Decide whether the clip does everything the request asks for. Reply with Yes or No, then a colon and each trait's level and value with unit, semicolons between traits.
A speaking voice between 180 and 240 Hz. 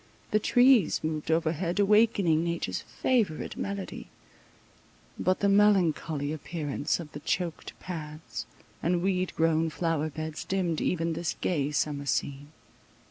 No: medium, 165 Hz